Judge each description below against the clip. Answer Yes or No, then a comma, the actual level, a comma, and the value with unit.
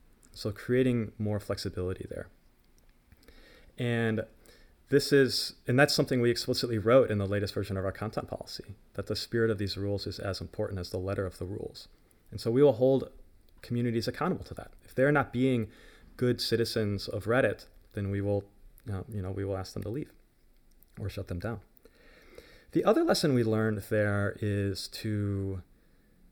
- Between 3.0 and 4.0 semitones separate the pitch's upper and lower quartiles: Yes, average, 3.3 semitones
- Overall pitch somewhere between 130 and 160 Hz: No, low, 105 Hz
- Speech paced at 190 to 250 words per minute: No, average, 180 wpm